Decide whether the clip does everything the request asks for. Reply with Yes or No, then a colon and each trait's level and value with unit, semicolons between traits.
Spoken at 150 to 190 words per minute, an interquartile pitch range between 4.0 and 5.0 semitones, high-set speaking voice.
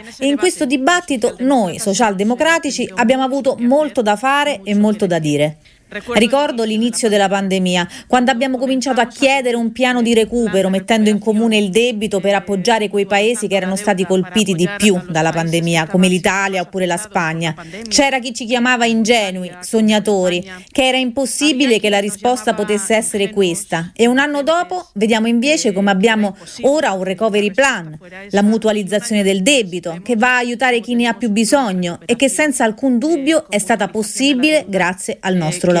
Yes: fast, 170 wpm; average, 4.6 semitones; high, 220 Hz